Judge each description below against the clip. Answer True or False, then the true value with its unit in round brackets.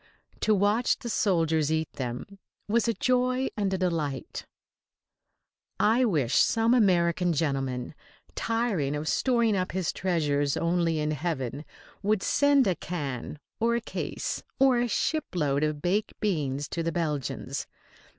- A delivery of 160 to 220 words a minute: False (140 wpm)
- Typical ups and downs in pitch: False (6.7 semitones)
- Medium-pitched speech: True (175 Hz)